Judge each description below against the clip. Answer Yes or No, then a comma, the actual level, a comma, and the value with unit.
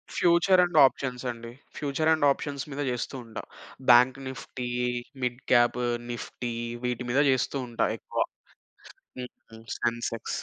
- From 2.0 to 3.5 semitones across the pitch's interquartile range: Yes, average, 2.9 semitones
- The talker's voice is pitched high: No, low, 125 Hz